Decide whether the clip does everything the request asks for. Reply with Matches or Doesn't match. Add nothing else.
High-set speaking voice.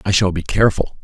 Doesn't match